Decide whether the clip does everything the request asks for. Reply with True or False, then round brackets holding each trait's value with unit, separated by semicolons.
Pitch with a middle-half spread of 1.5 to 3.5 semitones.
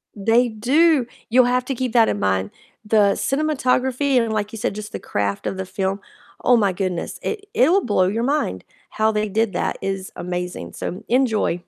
False (4.8 semitones)